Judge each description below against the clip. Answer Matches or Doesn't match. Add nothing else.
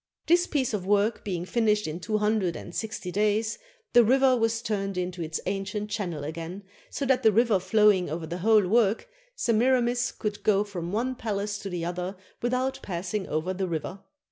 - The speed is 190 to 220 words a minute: Matches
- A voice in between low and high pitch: Doesn't match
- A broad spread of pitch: Doesn't match